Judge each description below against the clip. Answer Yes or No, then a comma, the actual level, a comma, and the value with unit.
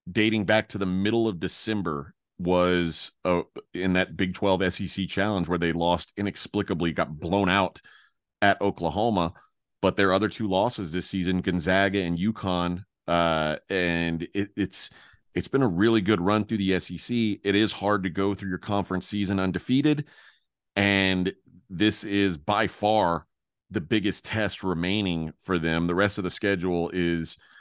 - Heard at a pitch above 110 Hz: No, very low, 95 Hz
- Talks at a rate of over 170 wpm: No, average, 160 wpm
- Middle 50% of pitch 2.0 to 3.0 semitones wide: Yes, narrow, 2.5 semitones